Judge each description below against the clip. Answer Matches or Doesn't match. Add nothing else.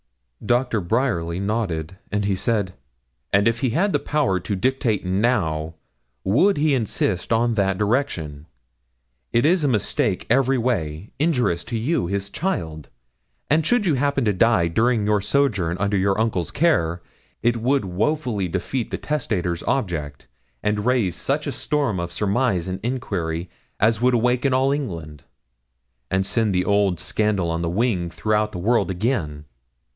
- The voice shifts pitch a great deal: Matches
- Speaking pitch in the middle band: Doesn't match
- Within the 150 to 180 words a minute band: Matches